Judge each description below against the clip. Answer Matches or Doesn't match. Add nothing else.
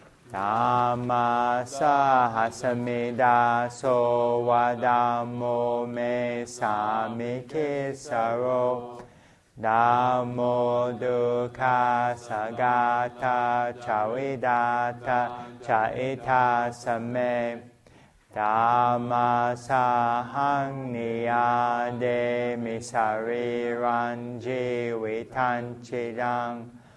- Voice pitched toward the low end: Matches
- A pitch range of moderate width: Doesn't match